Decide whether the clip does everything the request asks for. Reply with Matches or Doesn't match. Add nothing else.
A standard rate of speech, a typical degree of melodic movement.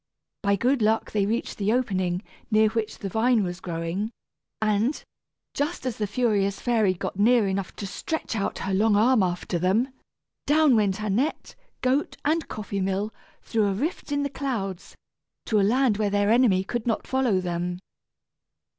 Matches